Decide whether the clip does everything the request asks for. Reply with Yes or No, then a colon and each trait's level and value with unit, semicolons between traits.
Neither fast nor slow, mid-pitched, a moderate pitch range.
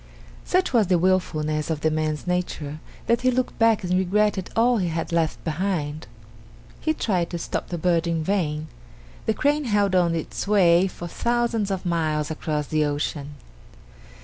Yes: average, 170 wpm; medium, 175 Hz; average, 4.8 semitones